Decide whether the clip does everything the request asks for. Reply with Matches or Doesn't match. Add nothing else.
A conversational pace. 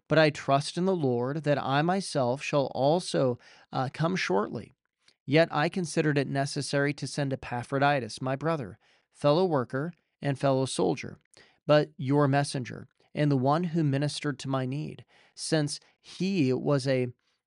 Matches